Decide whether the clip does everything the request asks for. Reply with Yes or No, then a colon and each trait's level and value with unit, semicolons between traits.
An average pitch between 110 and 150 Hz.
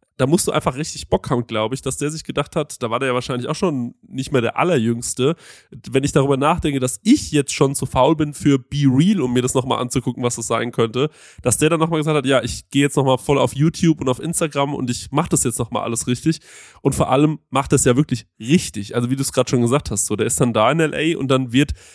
Yes: low, 135 Hz